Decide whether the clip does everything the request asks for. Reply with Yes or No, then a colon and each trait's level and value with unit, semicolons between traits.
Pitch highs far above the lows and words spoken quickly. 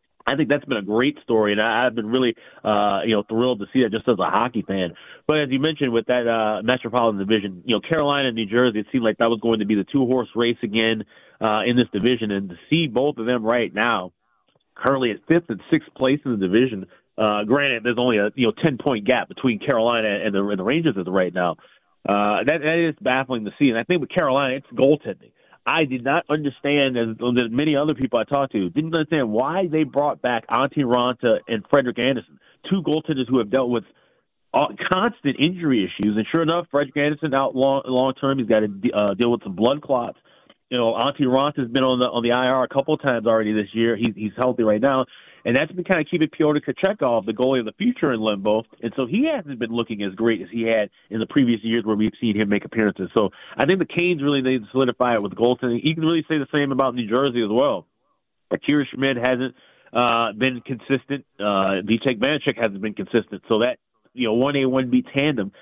No: average, 4.0 semitones; fast, 240 wpm